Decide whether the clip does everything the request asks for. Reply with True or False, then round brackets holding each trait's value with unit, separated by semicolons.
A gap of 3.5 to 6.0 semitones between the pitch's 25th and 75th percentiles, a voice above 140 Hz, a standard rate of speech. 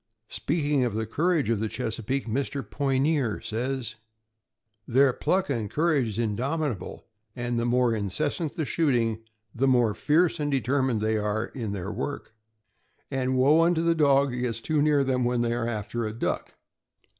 False (4.1 semitones; 125 Hz; 175 wpm)